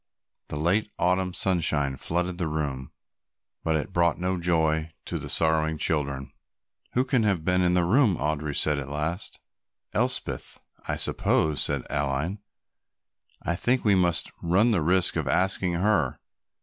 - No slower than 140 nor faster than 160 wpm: Yes, average, 150 wpm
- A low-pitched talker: Yes, very low, 85 Hz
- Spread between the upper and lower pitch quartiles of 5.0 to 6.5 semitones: No, average, 3.4 semitones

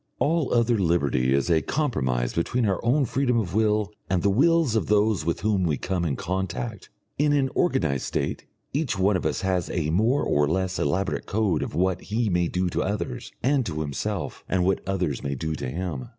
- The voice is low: Yes, very low, 95 Hz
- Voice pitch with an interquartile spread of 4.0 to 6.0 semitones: Yes, wide, 5.6 semitones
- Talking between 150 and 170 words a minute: No, fast, 205 wpm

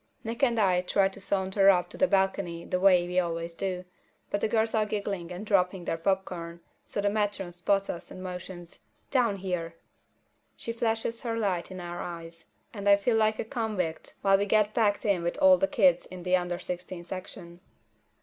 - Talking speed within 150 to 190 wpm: No, average, 200 wpm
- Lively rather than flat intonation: No, average, 3.0 semitones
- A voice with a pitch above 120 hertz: Yes, high, 190 Hz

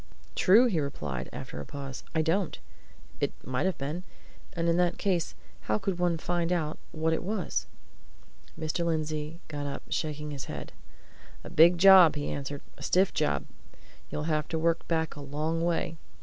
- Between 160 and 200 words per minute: Yes, average, 175 wpm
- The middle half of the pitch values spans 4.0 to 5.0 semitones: No, average, 2.9 semitones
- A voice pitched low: No, medium, 160 Hz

